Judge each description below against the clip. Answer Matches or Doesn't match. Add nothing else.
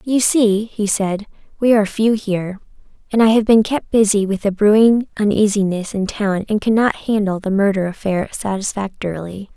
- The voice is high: Matches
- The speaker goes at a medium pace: Matches